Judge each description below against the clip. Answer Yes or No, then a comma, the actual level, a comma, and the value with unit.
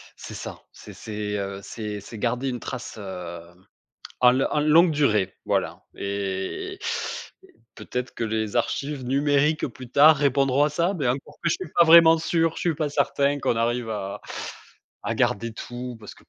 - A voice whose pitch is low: Yes, low, 125 Hz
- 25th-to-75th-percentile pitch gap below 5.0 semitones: No, wide, 5.6 semitones